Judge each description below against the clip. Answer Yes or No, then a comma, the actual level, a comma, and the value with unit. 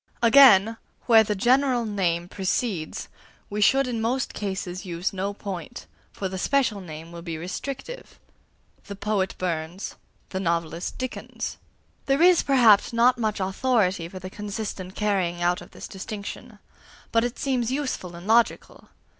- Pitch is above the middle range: Yes, high, 205 Hz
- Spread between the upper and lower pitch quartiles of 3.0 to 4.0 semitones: No, average, 4.7 semitones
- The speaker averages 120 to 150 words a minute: Yes, average, 145 wpm